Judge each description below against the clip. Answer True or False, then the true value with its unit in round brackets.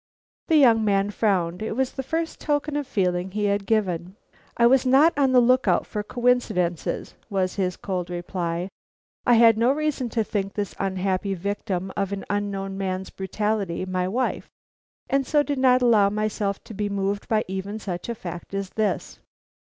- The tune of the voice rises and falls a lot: False (4.2 semitones)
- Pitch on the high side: True (205 Hz)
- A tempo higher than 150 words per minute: True (180 wpm)